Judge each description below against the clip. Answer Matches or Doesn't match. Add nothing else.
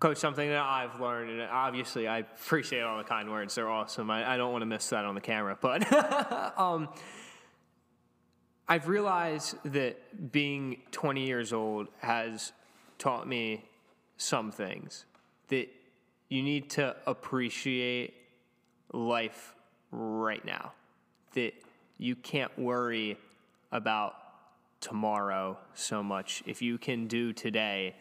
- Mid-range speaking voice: Doesn't match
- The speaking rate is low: Matches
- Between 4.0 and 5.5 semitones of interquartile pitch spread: Matches